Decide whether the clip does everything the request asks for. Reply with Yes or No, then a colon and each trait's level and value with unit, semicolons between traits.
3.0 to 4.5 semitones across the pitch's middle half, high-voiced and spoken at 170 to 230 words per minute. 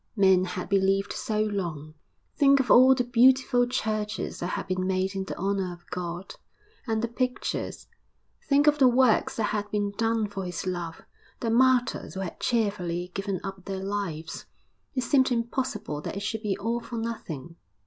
Yes: average, 4.1 semitones; high, 205 Hz; average, 180 wpm